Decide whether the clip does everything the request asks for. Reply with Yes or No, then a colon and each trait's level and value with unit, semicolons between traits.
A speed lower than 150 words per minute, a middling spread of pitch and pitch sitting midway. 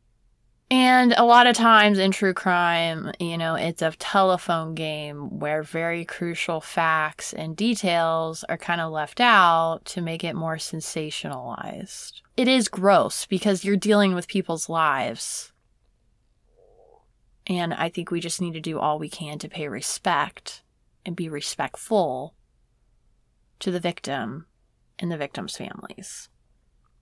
Yes: average, 140 wpm; average, 3.3 semitones; medium, 170 Hz